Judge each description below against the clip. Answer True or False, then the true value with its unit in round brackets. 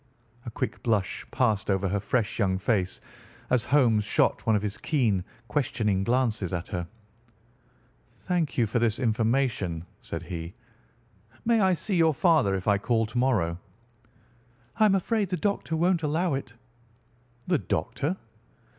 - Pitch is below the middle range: True (115 Hz)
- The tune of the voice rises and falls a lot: True (7.5 semitones)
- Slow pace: False (150 wpm)